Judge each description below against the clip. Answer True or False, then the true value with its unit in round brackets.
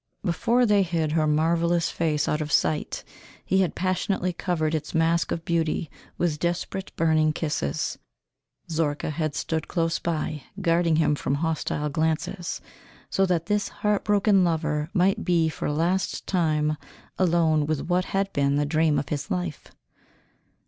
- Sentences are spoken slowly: False (150 wpm)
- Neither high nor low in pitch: True (165 Hz)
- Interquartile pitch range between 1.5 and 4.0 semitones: True (2.6 semitones)